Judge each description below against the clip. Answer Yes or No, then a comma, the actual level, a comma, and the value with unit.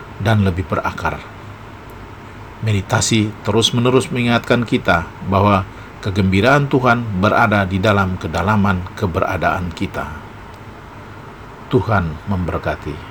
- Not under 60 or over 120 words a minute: Yes, slow, 85 wpm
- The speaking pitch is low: Yes, low, 105 Hz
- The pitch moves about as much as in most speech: Yes, average, 3.0 semitones